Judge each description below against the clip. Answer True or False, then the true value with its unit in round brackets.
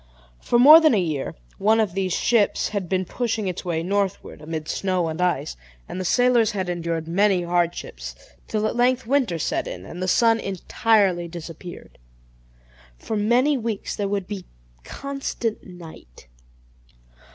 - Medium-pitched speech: False (195 Hz)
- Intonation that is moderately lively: True (4.6 semitones)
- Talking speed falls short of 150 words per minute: False (155 wpm)